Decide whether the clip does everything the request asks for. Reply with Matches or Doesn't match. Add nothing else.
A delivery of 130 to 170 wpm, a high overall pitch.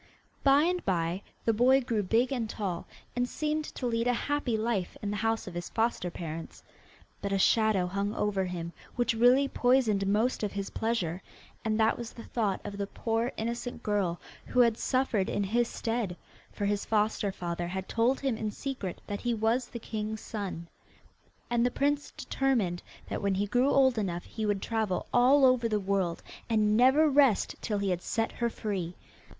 Doesn't match